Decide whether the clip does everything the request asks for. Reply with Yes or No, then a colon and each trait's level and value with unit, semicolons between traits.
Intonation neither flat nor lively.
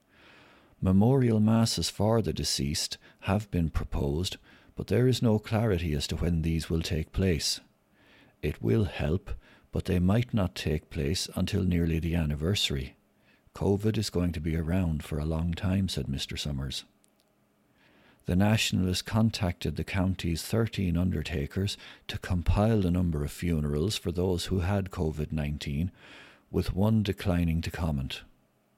Yes: average, 3.9 semitones